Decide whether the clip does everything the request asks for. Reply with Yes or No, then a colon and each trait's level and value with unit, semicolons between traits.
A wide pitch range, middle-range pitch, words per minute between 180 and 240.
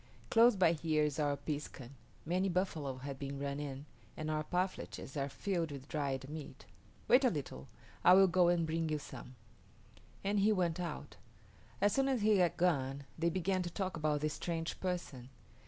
No: average, 4.5 semitones; medium, 160 Hz; average, 185 wpm